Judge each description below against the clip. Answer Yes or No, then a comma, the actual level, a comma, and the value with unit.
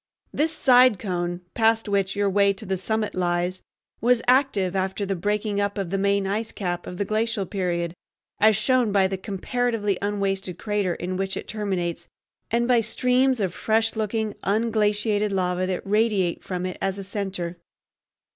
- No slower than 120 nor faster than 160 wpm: No, average, 170 wpm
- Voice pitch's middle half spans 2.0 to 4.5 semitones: Yes, average, 2.8 semitones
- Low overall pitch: No, high, 200 Hz